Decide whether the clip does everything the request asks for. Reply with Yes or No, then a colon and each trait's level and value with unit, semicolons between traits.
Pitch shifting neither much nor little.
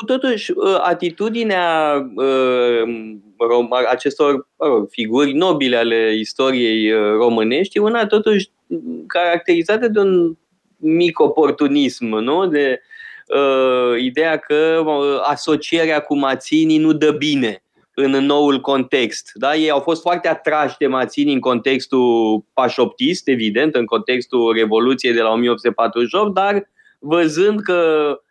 No: wide, 5.7 semitones